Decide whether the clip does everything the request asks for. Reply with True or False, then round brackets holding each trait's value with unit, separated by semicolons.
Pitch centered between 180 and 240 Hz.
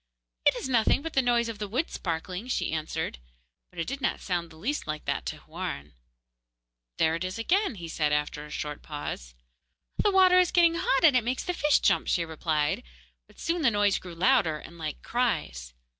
True (190 Hz)